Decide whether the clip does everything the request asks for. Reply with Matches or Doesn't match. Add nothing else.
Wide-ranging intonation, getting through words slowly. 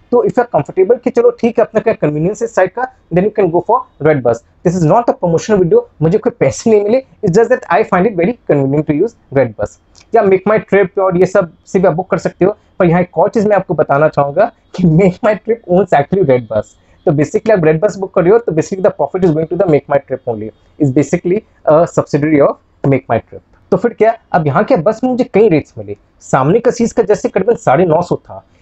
Doesn't match